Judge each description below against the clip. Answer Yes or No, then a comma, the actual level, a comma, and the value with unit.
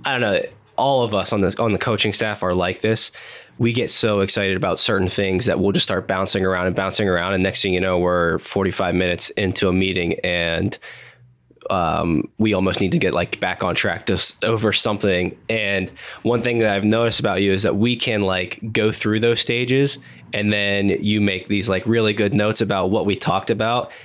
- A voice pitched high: No, low, 100 Hz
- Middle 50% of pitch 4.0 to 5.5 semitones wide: No, average, 2.9 semitones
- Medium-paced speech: No, fast, 220 wpm